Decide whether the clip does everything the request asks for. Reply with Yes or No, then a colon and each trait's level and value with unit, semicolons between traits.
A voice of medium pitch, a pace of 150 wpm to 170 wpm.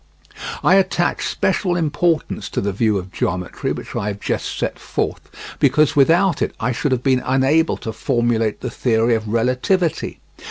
No: low, 125 Hz; average, 165 wpm